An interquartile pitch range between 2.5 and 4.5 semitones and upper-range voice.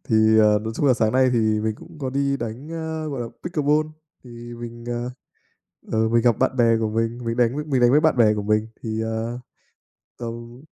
No: average, 3.1 semitones; low, 120 Hz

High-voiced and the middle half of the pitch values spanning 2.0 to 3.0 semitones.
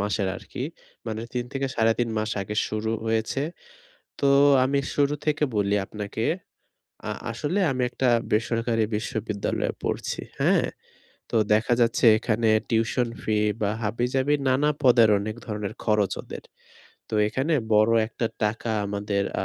No: low, 115 Hz; average, 2.7 semitones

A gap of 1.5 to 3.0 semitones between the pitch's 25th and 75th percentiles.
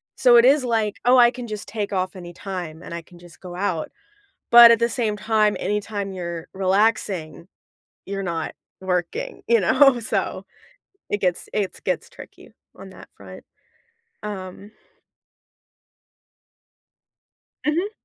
No: average, 4.5 semitones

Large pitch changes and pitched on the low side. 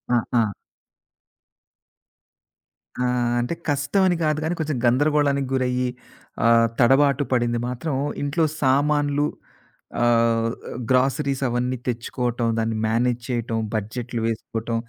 No: average, 3.3 semitones; low, 125 Hz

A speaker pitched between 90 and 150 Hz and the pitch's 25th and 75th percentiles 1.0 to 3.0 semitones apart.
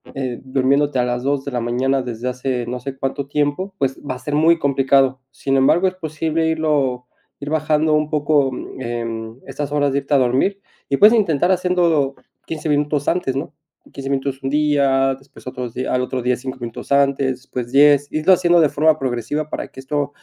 Yes: medium, 140 Hz; average, 2.7 semitones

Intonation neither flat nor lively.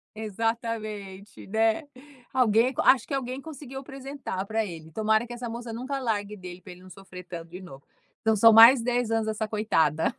Yes: average, 3.9 semitones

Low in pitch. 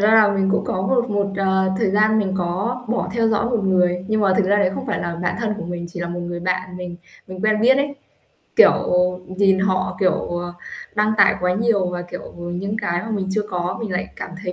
No: high, 190 Hz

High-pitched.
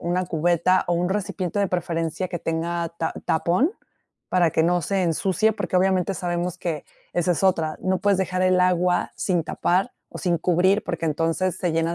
No: medium, 180 Hz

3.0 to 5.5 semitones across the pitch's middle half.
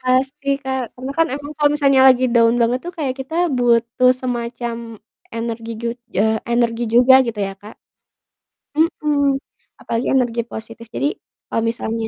No: narrow, 2.4 semitones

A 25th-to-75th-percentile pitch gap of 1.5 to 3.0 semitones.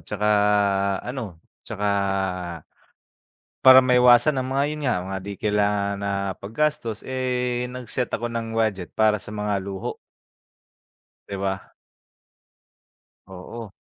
No: average, 3.8 semitones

